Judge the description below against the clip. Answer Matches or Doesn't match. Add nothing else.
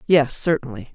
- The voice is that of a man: Doesn't match